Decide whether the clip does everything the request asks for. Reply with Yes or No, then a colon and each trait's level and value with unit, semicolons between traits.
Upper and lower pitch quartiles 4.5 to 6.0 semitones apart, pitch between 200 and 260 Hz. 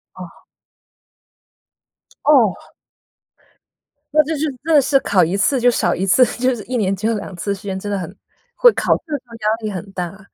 Yes: average, 5.0 semitones; high, 215 Hz